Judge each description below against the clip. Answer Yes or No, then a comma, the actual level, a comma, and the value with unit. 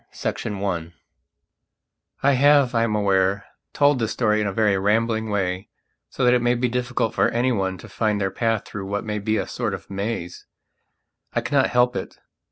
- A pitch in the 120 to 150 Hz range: No, low, 110 Hz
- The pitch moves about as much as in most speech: Yes, average, 3.6 semitones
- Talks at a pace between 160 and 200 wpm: Yes, average, 190 wpm